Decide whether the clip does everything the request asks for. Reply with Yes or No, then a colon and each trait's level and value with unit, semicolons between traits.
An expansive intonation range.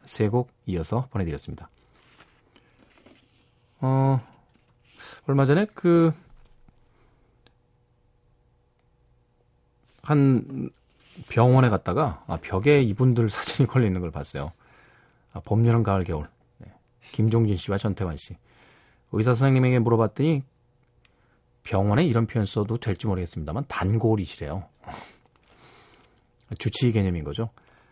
No: average, 3.8 semitones